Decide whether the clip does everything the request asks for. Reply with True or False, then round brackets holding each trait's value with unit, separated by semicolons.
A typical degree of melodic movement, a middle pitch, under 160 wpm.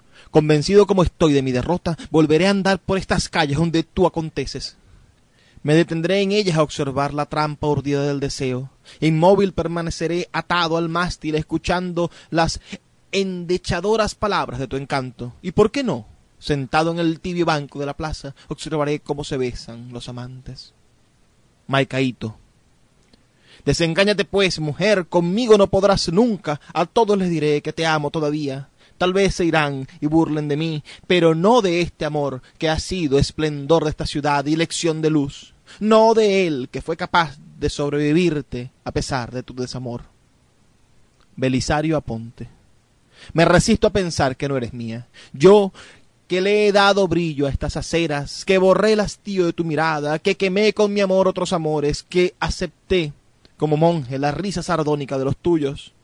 False (4.2 semitones; 155 Hz; 165 wpm)